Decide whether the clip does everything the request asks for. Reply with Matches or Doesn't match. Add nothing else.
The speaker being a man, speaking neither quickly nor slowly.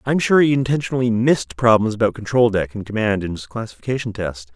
Matches